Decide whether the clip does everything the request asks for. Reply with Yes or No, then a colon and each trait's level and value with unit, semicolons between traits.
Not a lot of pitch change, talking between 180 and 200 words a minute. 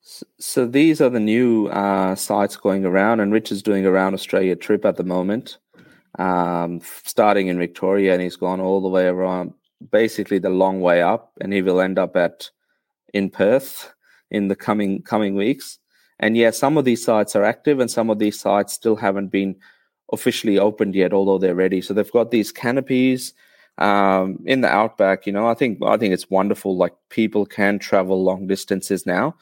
Yes: narrow, 2.1 semitones; average, 195 wpm